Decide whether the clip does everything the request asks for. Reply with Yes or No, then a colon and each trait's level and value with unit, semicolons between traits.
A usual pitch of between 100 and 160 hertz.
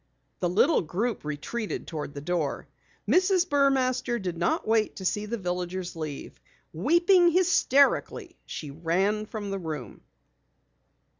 No: high, 205 Hz